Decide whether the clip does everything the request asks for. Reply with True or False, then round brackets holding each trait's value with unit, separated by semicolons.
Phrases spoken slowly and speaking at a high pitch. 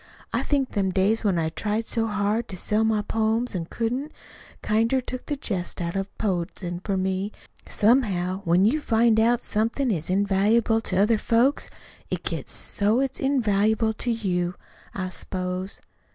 False (165 wpm; 210 Hz)